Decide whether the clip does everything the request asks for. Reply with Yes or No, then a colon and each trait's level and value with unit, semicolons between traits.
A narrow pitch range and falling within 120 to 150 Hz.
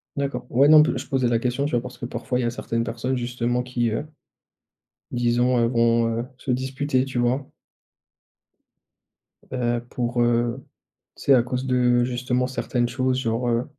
Yes: narrow, 1.3 semitones; low, 125 Hz